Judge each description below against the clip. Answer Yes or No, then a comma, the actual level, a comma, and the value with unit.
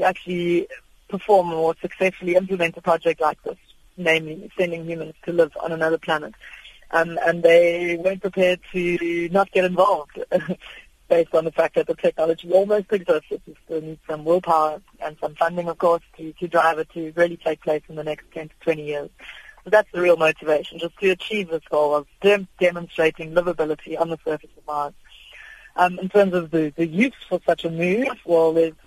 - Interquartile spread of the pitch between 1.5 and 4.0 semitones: Yes, narrow, 2.4 semitones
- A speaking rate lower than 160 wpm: No, average, 195 wpm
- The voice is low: No, medium, 170 Hz